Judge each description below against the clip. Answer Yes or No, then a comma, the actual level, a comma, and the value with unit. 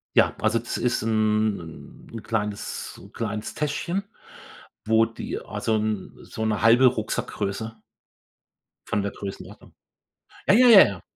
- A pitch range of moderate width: No, narrow, 1.6 semitones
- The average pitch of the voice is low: Yes, low, 110 Hz